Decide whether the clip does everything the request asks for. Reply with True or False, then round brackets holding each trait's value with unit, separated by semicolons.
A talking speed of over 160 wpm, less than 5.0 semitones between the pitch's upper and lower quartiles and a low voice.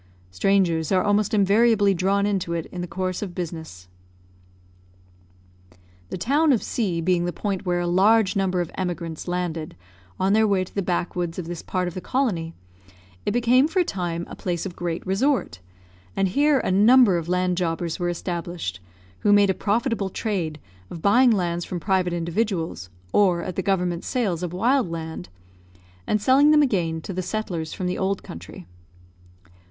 False (175 wpm; 3.1 semitones; 185 Hz)